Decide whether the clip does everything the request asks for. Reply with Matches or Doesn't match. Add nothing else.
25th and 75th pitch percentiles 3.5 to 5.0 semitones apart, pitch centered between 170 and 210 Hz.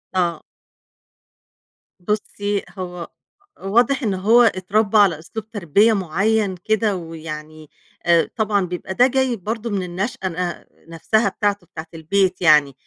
Matches